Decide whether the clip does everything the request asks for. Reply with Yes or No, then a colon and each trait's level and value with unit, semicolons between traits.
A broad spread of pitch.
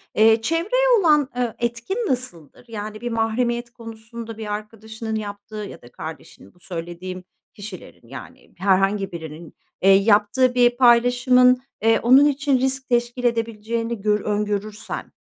No: average, 3.1 semitones